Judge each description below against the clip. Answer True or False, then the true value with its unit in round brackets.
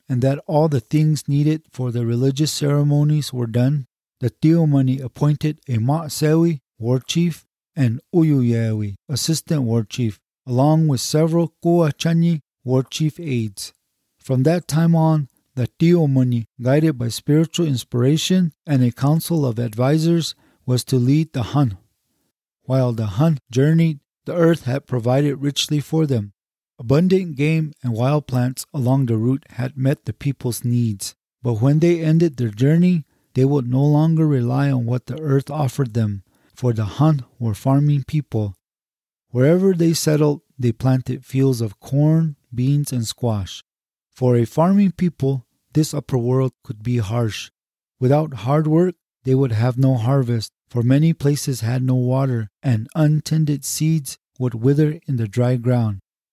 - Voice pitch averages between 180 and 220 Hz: False (135 Hz)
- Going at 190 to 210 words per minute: False (150 wpm)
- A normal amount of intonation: True (3.8 semitones)